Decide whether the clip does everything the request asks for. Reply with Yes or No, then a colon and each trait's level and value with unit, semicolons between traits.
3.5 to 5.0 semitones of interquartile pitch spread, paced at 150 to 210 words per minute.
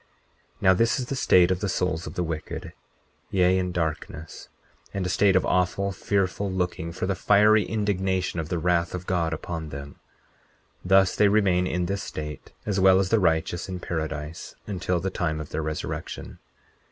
No: average, 2.7 semitones; average, 185 wpm